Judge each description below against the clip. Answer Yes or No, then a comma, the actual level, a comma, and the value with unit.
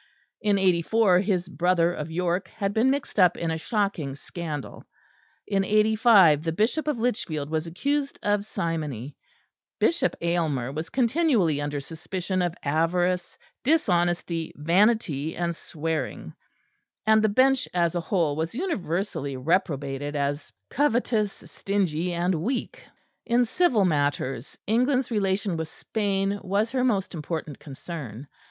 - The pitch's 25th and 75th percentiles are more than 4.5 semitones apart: Yes, average, 5.2 semitones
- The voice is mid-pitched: Yes, medium, 180 Hz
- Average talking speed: No, slow, 130 wpm